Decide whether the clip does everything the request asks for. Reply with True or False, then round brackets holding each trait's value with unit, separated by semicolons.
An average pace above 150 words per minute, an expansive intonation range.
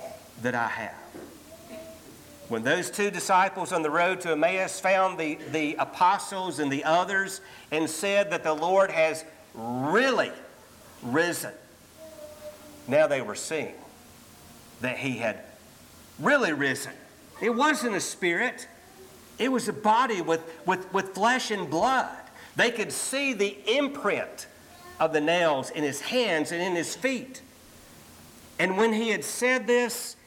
False (140 wpm; 6.8 semitones)